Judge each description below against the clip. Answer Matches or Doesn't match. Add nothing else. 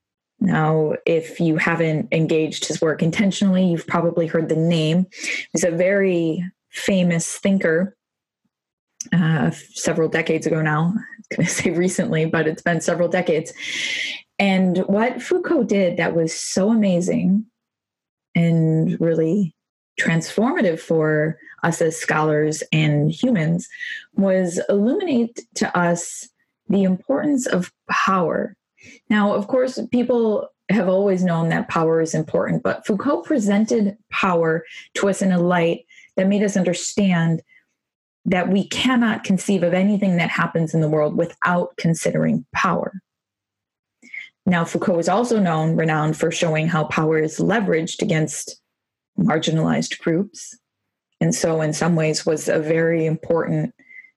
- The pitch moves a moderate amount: Matches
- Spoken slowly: Matches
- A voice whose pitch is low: Doesn't match